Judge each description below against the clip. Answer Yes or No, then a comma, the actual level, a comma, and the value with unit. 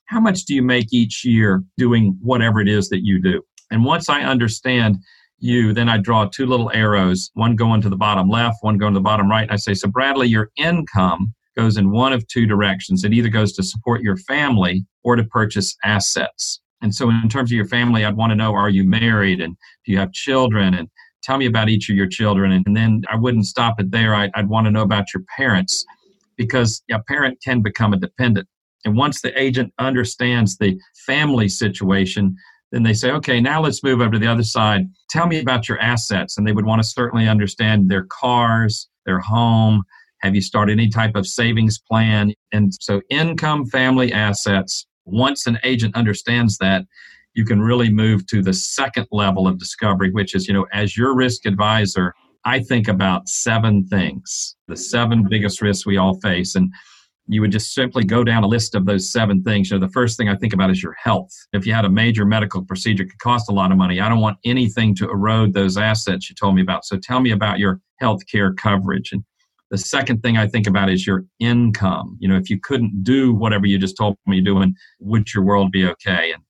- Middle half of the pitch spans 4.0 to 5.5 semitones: No, average, 3.2 semitones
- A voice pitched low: Yes, low, 110 Hz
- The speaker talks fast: Yes, fast, 220 wpm